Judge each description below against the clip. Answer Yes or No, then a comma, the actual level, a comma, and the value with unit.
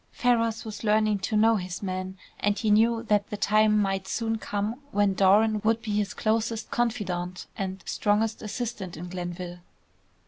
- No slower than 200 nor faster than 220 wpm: No, average, 165 wpm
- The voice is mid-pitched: No, high, 210 Hz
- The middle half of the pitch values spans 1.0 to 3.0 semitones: Yes, average, 2.7 semitones